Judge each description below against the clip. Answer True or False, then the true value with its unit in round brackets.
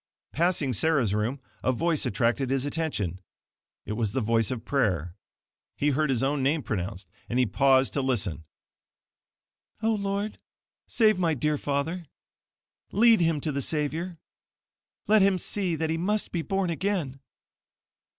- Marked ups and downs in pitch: True (5.9 semitones)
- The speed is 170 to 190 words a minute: False (150 wpm)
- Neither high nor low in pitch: True (145 Hz)